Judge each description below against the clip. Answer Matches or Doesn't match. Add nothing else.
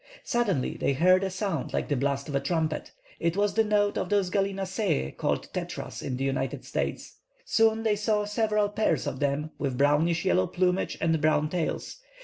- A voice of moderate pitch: Matches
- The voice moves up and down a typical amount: Doesn't match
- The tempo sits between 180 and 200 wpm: Matches